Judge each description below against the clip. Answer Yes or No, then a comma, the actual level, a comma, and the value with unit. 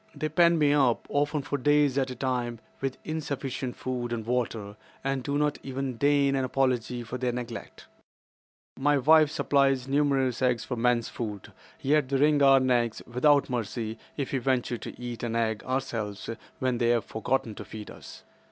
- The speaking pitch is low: Yes, low, 130 Hz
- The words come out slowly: No, average, 180 wpm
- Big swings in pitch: No, average, 2.9 semitones